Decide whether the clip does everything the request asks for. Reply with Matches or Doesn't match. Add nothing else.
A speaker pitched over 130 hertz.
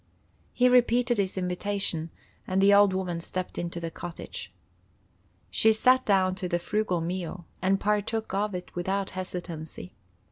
Matches